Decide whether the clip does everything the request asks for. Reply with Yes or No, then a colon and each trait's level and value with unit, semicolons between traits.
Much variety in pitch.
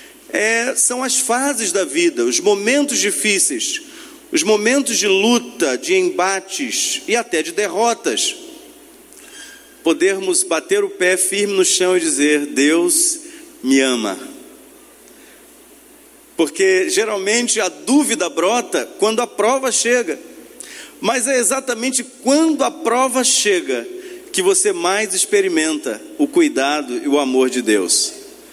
Yes: wide, 8.2 semitones